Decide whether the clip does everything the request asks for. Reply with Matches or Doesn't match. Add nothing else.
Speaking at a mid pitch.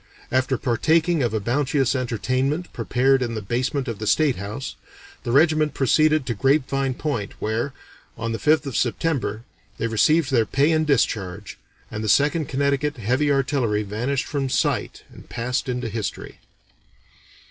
Doesn't match